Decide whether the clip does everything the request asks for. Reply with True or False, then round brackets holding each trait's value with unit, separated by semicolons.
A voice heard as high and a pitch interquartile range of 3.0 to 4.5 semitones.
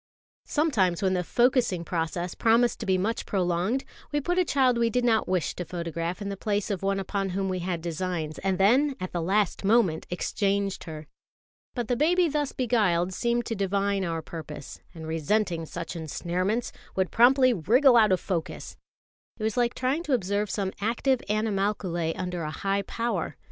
False (195 Hz; 5.0 semitones)